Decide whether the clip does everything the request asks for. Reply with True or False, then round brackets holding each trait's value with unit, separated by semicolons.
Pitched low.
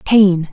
False (190 Hz)